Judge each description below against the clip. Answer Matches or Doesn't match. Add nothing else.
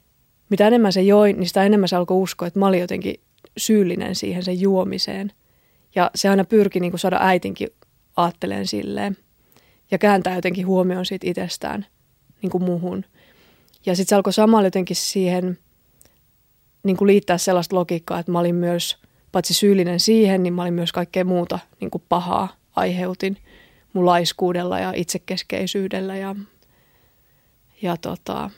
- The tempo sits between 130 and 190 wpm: Matches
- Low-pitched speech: Doesn't match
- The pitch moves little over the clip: Matches